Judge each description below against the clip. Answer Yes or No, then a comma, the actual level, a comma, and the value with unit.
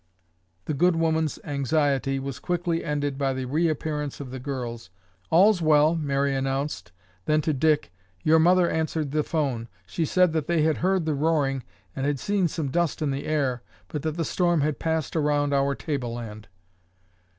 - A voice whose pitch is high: No, medium, 150 Hz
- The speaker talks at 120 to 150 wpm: No, average, 175 wpm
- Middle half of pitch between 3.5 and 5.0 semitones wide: No, average, 2.8 semitones